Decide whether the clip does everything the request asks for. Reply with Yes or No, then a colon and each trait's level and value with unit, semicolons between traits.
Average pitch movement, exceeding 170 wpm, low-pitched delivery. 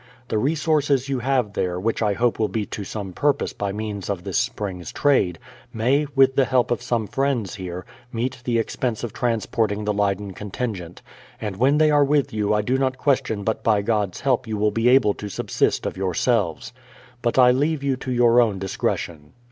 Yes: average, 4.3 semitones; average, 200 wpm; low, 115 Hz